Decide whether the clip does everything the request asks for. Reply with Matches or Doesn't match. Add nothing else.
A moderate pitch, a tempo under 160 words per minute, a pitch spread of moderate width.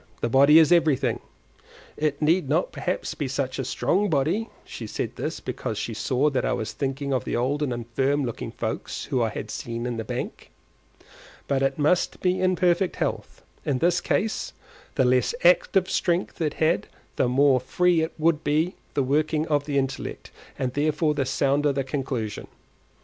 Doesn't match